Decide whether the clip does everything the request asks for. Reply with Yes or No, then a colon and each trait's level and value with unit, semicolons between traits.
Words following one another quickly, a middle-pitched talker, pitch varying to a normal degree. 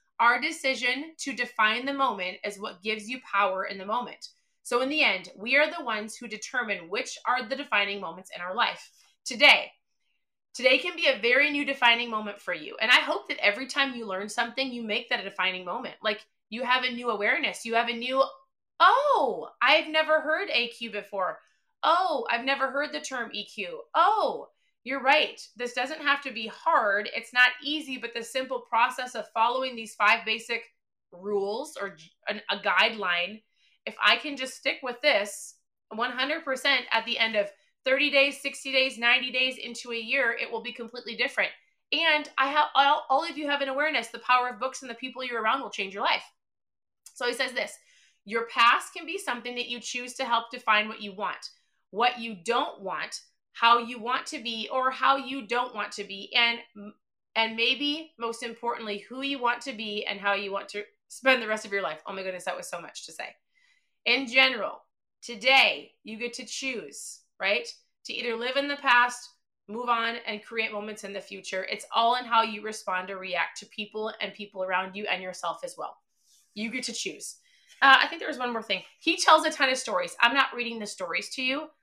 No: fast, 210 wpm; high, 240 Hz; average, 3.7 semitones